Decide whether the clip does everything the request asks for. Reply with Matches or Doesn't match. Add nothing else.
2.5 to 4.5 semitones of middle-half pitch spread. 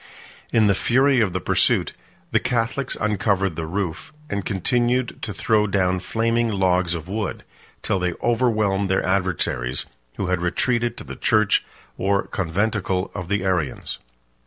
Matches